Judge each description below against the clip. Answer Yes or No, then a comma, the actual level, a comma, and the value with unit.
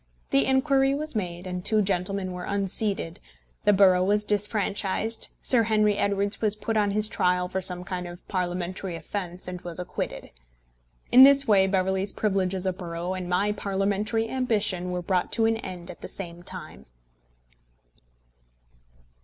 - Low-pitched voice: No, high, 195 Hz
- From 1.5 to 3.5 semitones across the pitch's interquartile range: Yes, average, 2.7 semitones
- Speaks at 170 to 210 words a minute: No, average, 160 wpm